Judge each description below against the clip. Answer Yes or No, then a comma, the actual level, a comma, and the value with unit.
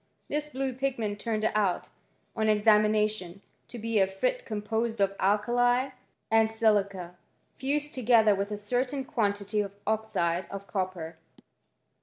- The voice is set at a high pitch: Yes, high, 215 Hz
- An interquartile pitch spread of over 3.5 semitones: No, average, 3.2 semitones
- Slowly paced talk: Yes, slow, 105 wpm